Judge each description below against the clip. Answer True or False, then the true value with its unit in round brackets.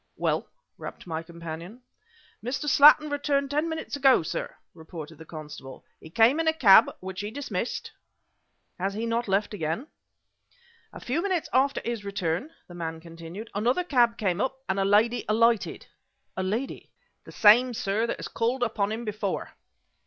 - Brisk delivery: False (165 wpm)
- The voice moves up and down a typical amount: False (6.1 semitones)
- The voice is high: True (220 Hz)